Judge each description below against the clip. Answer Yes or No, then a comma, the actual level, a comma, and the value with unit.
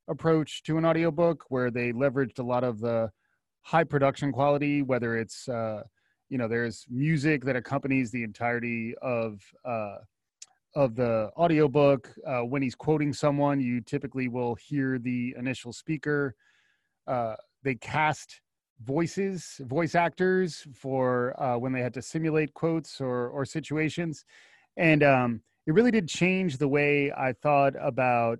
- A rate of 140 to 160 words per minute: Yes, average, 150 wpm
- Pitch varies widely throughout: No, average, 4.0 semitones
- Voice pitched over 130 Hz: Yes, medium, 140 Hz